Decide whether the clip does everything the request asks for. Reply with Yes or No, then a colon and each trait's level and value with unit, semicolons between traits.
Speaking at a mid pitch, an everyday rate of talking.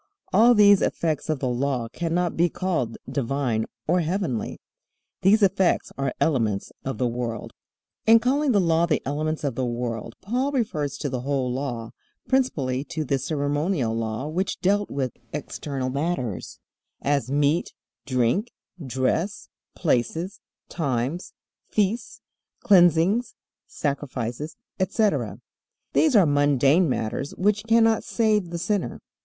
No: medium, 150 Hz; slow, 130 wpm